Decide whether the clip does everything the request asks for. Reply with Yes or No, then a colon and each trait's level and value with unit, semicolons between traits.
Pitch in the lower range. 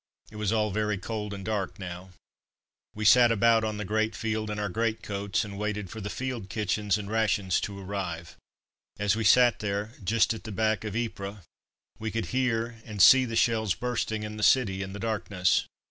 Yes: low, 105 Hz